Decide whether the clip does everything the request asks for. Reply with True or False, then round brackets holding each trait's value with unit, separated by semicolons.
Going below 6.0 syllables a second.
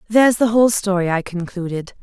False (6.1 syllables/s)